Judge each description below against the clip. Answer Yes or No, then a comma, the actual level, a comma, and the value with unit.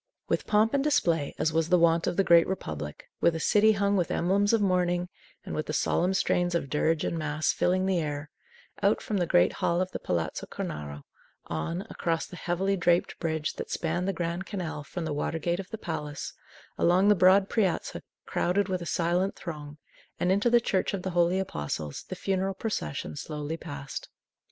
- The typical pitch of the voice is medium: Yes, medium, 175 Hz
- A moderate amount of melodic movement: Yes, average, 3.4 semitones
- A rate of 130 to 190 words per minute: No, average, 200 wpm